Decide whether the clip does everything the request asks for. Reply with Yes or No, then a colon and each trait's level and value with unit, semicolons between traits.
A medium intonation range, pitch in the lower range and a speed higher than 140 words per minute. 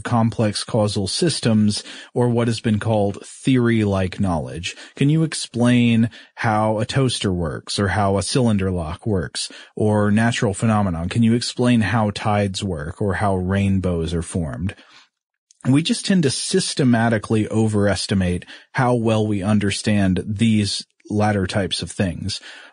No: average, 3.1 semitones; low, 105 Hz; slow, 135 wpm